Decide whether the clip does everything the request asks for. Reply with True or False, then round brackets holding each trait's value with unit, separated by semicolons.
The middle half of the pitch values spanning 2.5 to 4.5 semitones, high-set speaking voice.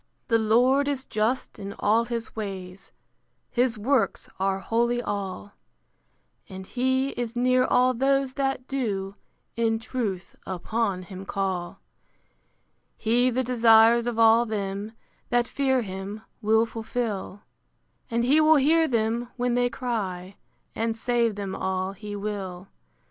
True (3.8 semitones; 225 Hz)